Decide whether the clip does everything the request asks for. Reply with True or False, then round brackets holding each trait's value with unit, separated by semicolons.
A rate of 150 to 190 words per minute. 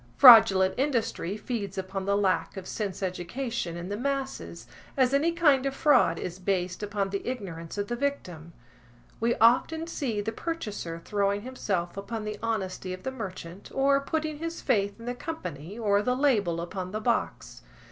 True (170 wpm)